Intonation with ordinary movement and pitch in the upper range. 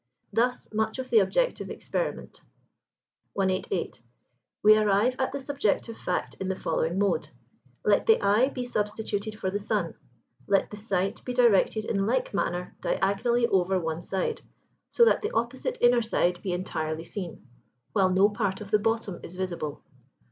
Yes: average, 4.0 semitones; high, 205 Hz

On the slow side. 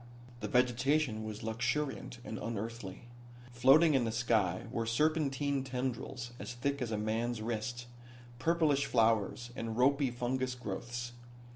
Yes: slow, 130 wpm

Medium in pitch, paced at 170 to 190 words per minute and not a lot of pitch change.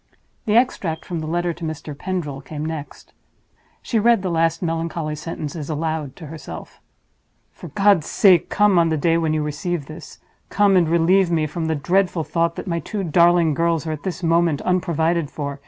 Yes: medium, 165 Hz; average, 185 wpm; narrow, 2.2 semitones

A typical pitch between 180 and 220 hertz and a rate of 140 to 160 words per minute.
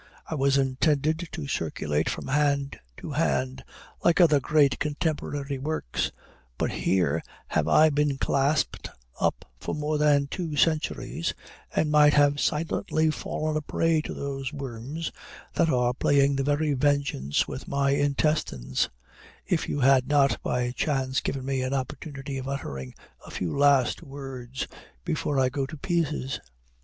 No: medium, 140 Hz; average, 150 wpm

